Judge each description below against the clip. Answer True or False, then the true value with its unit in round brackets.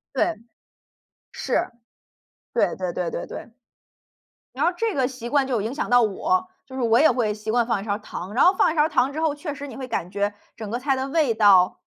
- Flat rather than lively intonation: False (5.2 semitones)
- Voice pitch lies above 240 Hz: True (250 Hz)